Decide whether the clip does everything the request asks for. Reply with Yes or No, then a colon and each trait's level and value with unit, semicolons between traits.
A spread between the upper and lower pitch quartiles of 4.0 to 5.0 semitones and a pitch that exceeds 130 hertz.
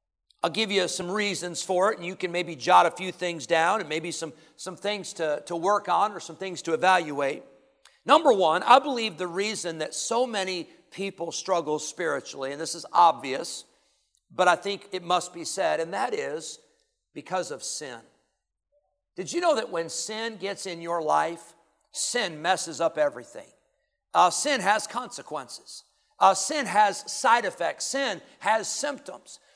Yes: average, 4.5 semitones; medium, 185 Hz